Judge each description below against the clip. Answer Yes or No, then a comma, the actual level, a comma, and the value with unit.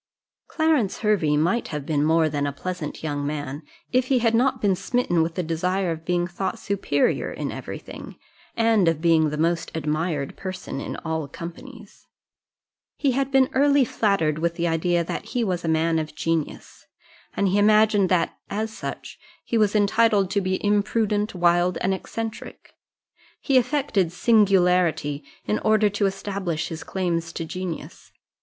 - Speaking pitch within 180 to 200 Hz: Yes, medium, 185 Hz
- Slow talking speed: No, average, 165 wpm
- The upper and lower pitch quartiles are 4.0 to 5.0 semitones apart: Yes, average, 4.6 semitones